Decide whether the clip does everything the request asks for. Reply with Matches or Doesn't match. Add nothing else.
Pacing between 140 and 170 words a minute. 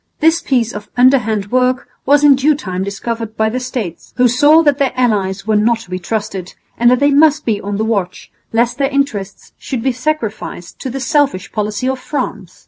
Doesn't match